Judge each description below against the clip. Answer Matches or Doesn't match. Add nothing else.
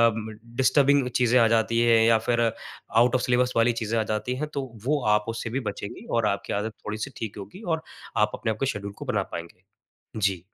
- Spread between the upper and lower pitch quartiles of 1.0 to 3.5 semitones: Matches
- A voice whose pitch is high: Doesn't match